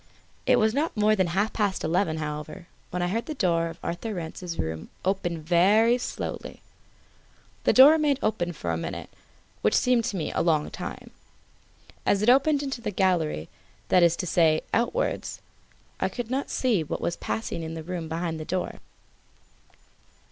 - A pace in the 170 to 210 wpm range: Yes, average, 175 wpm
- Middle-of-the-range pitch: Yes, medium, 180 Hz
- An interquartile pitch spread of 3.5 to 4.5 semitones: No, wide, 5.5 semitones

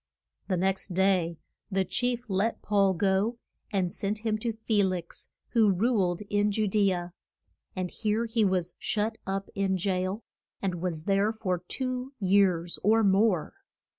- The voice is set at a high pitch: Yes, high, 195 Hz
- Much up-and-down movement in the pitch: No, average, 2.8 semitones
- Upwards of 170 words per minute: No, average, 155 wpm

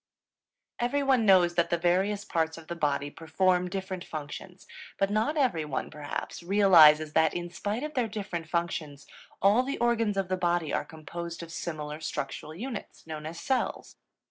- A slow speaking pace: No, average, 165 wpm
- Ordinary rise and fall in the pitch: Yes, average, 4.3 semitones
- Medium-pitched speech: Yes, medium, 175 Hz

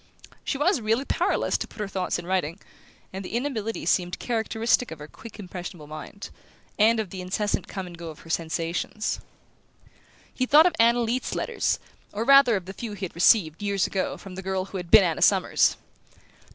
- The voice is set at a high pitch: Yes, high, 195 Hz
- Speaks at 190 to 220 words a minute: Yes, average, 195 wpm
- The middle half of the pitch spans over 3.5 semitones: Yes, average, 4.2 semitones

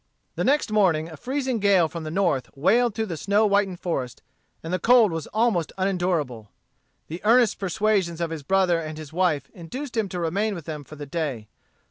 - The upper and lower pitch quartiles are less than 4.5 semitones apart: No, average, 4.9 semitones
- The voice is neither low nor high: Yes, medium, 180 Hz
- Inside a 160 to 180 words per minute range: No, average, 195 wpm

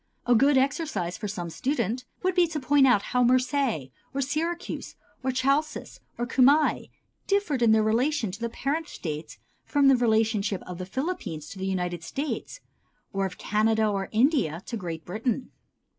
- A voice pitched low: No, high, 240 Hz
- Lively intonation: Yes, wide, 6.2 semitones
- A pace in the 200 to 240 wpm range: No, average, 170 wpm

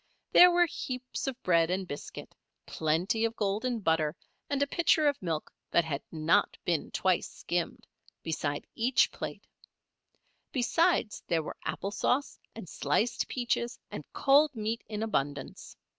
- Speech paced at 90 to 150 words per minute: Yes, average, 145 wpm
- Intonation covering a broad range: Yes, wide, 7.7 semitones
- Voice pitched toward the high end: Yes, high, 210 Hz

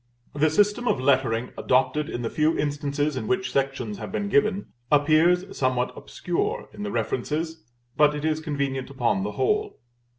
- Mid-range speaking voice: Yes, medium, 145 Hz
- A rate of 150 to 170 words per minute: Yes, average, 165 wpm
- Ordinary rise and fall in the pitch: Yes, average, 4.1 semitones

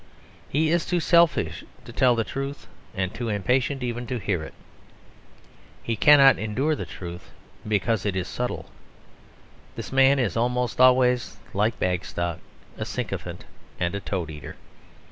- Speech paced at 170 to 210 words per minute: No, average, 145 wpm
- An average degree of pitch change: No, wide, 5.7 semitones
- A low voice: Yes, low, 120 Hz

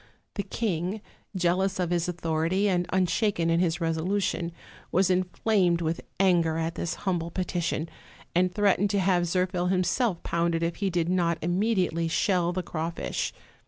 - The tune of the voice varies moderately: No, narrow, 2.0 semitones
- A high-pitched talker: No, medium, 180 Hz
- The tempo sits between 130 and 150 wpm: No, average, 160 wpm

